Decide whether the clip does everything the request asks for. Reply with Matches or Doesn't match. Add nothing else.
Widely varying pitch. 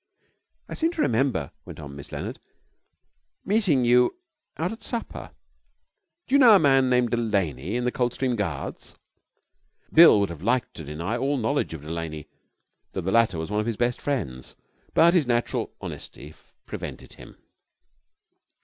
Matches